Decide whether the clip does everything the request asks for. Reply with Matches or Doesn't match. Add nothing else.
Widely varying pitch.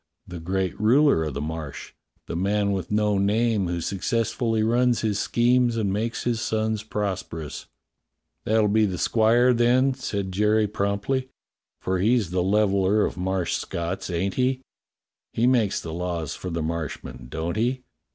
Doesn't match